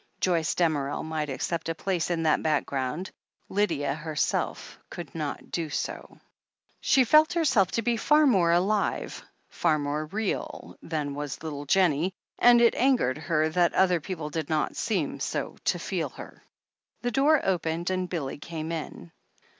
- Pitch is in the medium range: Yes, medium, 165 Hz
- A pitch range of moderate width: Yes, average, 4.0 semitones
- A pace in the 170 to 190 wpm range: No, average, 160 wpm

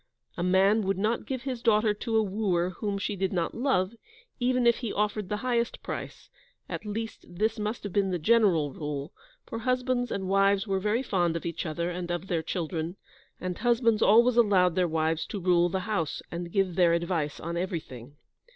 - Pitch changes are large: No, average, 4.3 semitones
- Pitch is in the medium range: No, high, 195 Hz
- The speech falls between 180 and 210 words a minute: Yes, average, 195 wpm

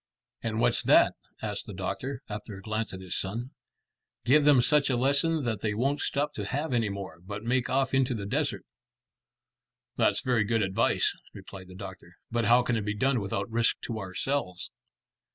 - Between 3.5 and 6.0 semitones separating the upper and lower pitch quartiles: Yes, average, 4.7 semitones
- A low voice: Yes, low, 115 Hz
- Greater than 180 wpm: Yes, average, 190 wpm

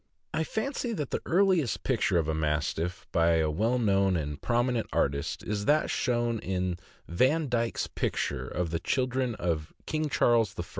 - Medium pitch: No, low, 110 Hz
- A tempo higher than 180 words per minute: No, average, 160 wpm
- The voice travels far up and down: Yes, wide, 7.3 semitones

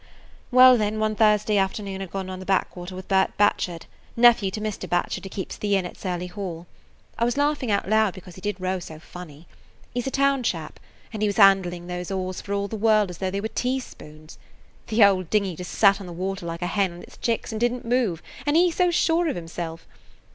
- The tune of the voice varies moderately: Yes, average, 3.4 semitones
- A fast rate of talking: Yes, fast, 235 wpm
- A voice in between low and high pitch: No, high, 195 Hz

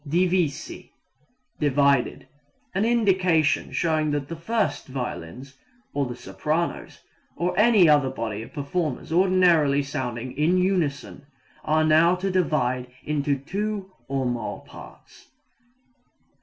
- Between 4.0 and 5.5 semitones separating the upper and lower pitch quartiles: Yes, average, 4.7 semitones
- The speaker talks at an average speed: No, slow, 115 wpm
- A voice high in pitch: No, medium, 155 Hz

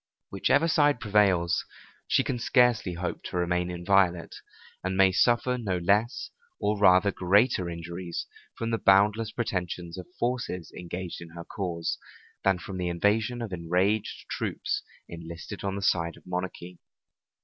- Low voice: Yes, very low, 95 Hz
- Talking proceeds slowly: No, average, 145 wpm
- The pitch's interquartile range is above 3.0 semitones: Yes, average, 3.5 semitones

